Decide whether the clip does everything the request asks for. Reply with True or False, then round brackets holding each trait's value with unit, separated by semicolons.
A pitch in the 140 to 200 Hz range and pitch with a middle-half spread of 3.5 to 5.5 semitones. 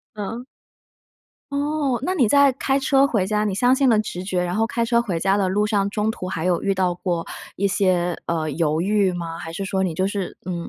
True (195 Hz; 4.5 semitones)